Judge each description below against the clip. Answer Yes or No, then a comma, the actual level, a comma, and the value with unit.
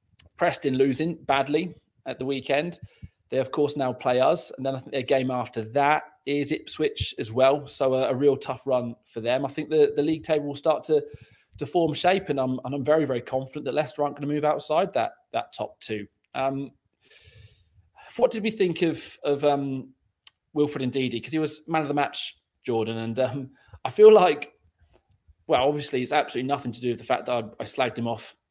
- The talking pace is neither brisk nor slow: No, fast, 215 wpm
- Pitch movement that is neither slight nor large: Yes, average, 3.2 semitones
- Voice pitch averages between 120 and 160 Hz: Yes, low, 135 Hz